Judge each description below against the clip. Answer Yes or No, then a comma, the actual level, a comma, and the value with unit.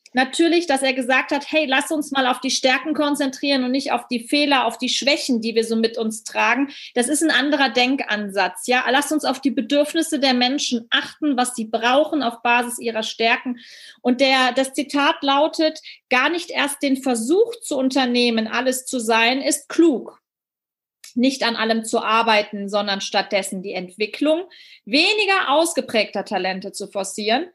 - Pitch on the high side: Yes, very high, 260 Hz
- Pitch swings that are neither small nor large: Yes, average, 4.1 semitones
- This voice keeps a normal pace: Yes, average, 170 wpm